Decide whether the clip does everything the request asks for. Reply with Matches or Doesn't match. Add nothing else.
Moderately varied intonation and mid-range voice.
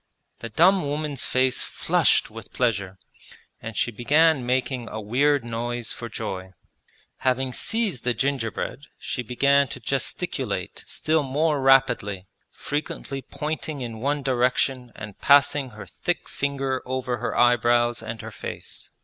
Doesn't match